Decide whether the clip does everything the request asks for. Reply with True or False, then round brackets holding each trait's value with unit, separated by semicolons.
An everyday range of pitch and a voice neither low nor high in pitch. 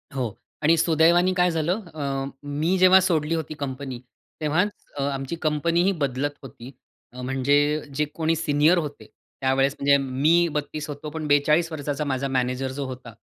True (3.2 semitones; 145 Hz)